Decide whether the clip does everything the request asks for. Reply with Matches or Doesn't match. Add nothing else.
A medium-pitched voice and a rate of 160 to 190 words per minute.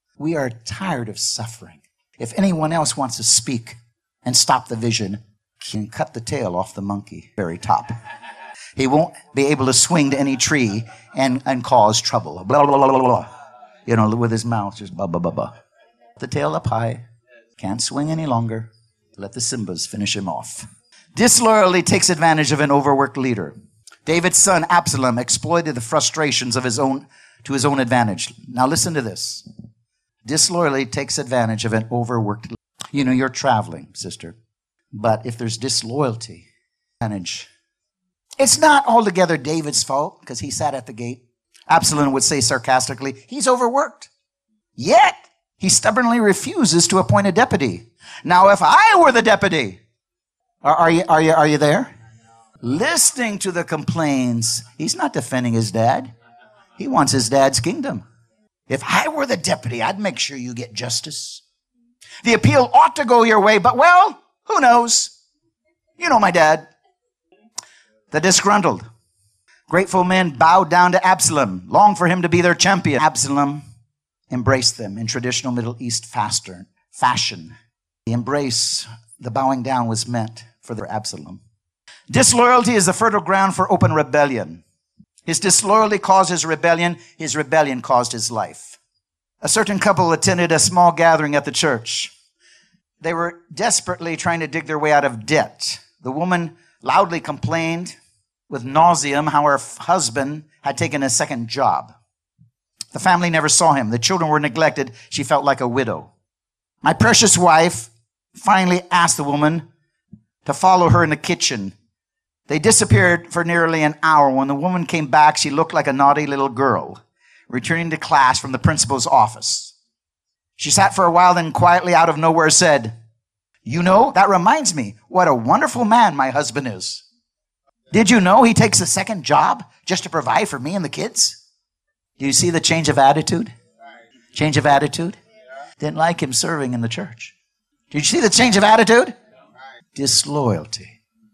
Matches